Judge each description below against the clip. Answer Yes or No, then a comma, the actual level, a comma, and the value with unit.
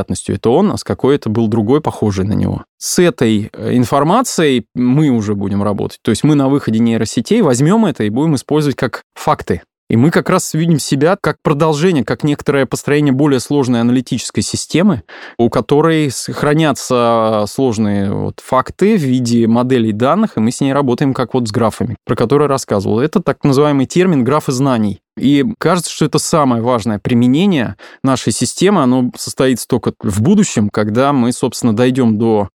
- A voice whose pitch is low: Yes, low, 130 Hz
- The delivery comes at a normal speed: No, fast, 170 wpm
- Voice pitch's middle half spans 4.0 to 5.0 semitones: Yes, average, 4.3 semitones